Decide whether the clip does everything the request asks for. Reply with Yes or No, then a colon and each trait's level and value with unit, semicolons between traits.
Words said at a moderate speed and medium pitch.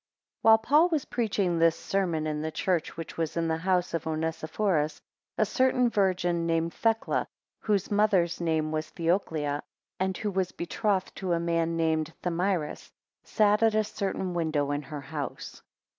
Yes: average, 160 wpm; medium, 170 Hz